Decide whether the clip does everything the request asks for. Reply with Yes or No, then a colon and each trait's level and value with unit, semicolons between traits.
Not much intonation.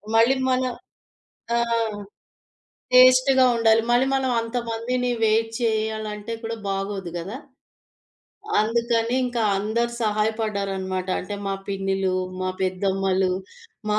No: average, 3.2 semitones